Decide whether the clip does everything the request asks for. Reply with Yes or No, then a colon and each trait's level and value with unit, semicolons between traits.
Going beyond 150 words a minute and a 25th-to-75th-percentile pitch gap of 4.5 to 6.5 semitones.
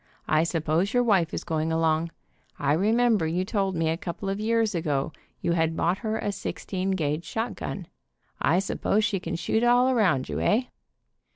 Yes: average, 180 wpm; average, 4.8 semitones